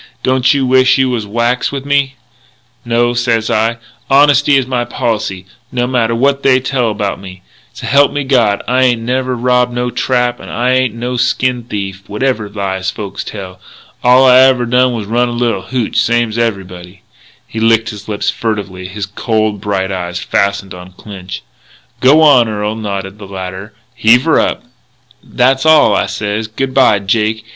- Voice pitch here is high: No, low, 115 Hz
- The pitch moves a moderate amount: Yes, average, 3.9 semitones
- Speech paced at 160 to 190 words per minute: Yes, average, 170 wpm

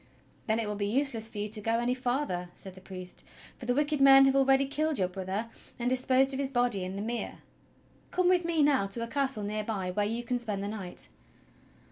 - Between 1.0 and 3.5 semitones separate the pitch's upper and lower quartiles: No, average, 4.8 semitones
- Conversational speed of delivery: No, fast, 230 wpm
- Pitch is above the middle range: Yes, high, 235 Hz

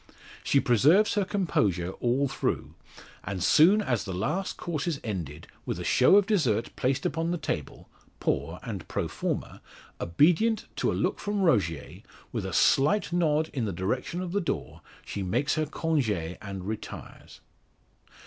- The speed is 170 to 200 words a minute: No, average, 160 wpm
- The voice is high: No, medium, 140 Hz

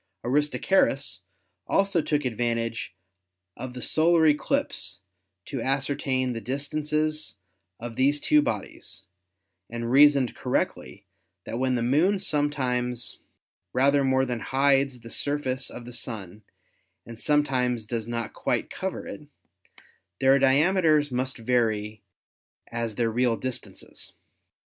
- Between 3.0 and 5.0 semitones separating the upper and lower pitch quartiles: Yes, average, 3.7 semitones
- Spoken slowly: Yes, slow, 120 wpm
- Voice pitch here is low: Yes, low, 130 Hz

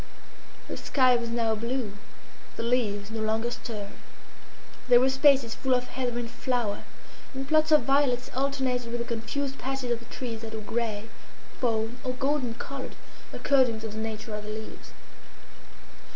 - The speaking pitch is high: Yes, high, 240 Hz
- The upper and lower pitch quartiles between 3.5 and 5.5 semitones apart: No, average, 2.9 semitones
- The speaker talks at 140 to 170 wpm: Yes, average, 165 wpm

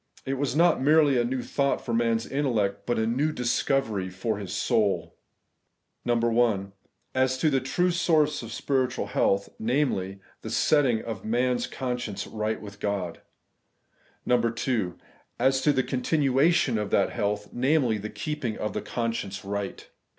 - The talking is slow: No, average, 160 wpm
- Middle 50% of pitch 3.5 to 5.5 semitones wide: Yes, average, 4.1 semitones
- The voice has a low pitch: Yes, low, 120 Hz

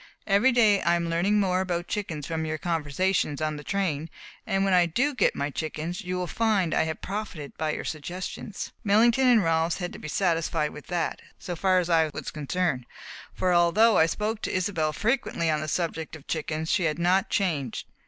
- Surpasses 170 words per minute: Yes, average, 200 wpm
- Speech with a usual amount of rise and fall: Yes, average, 3.8 semitones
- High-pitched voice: No, medium, 175 Hz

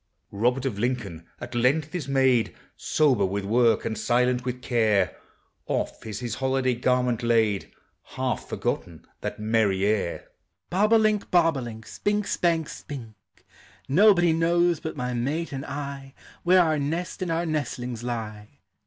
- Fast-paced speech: No, average, 155 wpm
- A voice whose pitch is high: No, low, 125 Hz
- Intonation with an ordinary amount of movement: No, wide, 5.8 semitones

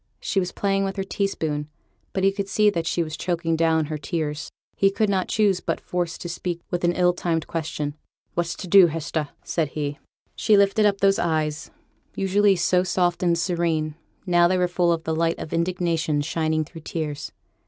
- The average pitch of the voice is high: No, medium, 175 Hz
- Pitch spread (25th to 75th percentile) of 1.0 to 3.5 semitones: Yes, average, 2.9 semitones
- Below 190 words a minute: No, average, 200 wpm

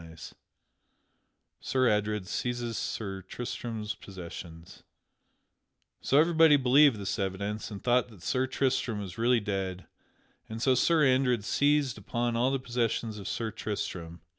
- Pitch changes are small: No, average, 4.2 semitones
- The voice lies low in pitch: Yes, low, 115 Hz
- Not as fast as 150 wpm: Yes, slow, 135 wpm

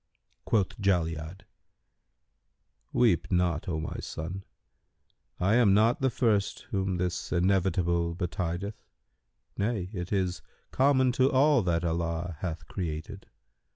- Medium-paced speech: No, slow, 115 wpm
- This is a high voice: No, very low, 90 Hz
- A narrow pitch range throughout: No, average, 3.4 semitones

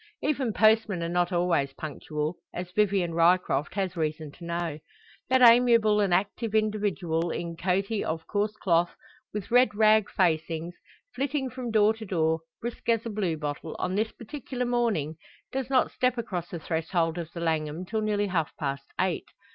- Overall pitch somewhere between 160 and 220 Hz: Yes, medium, 185 Hz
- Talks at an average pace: Yes, average, 170 wpm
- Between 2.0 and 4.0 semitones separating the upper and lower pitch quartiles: No, average, 4.9 semitones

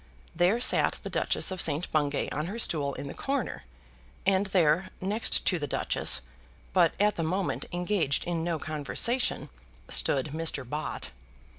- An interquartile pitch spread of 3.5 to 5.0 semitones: Yes, average, 4.3 semitones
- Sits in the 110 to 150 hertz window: No, medium, 170 Hz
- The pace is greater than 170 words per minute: No, average, 155 wpm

